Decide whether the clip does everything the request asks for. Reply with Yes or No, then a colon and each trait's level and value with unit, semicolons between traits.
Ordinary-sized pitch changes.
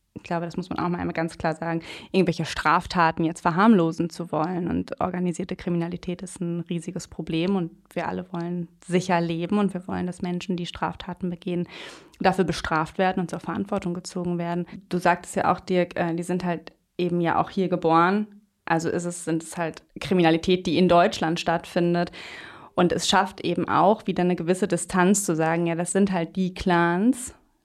No: narrow, 1.4 semitones